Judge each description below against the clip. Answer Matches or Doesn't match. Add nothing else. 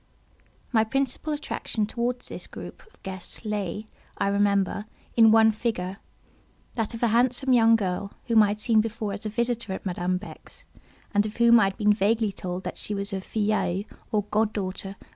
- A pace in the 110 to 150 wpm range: Doesn't match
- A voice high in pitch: Matches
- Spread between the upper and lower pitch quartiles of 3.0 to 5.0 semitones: Doesn't match